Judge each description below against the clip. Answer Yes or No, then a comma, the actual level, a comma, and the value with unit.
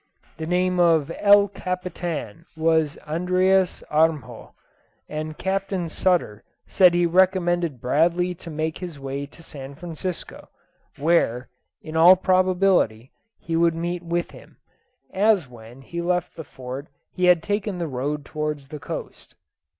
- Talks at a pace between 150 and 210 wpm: No, slow, 135 wpm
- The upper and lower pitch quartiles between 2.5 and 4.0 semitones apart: Yes, average, 3.3 semitones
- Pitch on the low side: No, medium, 170 Hz